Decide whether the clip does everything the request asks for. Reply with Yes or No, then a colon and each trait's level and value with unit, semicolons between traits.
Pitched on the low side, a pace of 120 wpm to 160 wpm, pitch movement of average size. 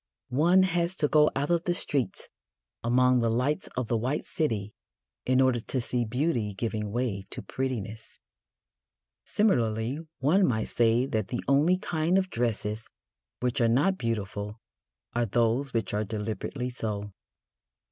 Yes: low, 120 Hz; average, 145 wpm; average, 4.6 semitones